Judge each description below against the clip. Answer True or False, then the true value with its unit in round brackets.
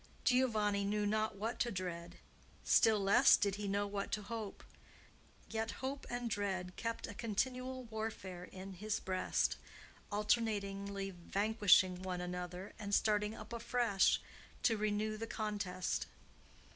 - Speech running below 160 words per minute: True (135 wpm)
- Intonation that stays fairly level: True (2.3 semitones)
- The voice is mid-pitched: False (205 Hz)